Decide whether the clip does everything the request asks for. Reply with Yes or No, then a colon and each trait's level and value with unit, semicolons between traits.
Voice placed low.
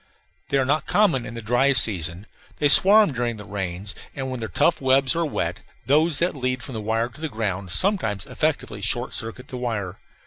Yes: low, 125 Hz